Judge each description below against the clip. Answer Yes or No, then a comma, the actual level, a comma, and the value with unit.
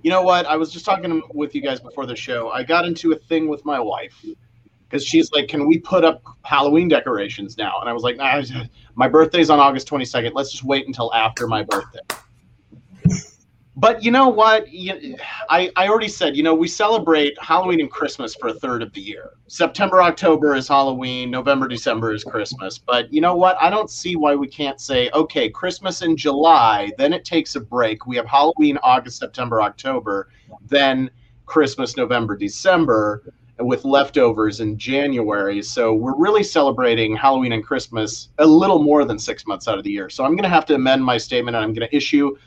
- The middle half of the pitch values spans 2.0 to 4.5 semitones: No, average, 5.1 semitones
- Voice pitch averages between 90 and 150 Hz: Yes, medium, 140 Hz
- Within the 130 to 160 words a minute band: No, average, 200 wpm